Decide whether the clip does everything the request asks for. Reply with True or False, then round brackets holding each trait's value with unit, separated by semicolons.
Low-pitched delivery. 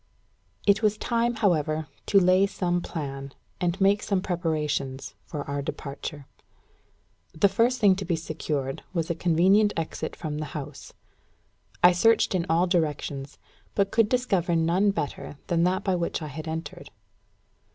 False (170 Hz)